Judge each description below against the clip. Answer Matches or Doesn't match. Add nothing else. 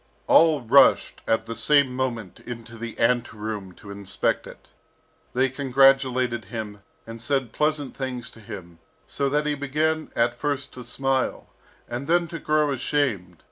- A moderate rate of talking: Matches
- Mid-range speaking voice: Doesn't match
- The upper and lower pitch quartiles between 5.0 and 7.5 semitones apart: Doesn't match